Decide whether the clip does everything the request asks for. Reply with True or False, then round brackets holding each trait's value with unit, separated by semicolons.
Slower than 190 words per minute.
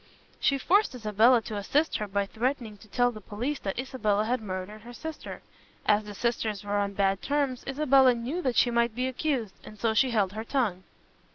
False (200 wpm)